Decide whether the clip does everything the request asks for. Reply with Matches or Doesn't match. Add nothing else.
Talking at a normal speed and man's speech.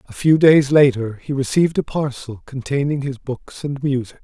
Matches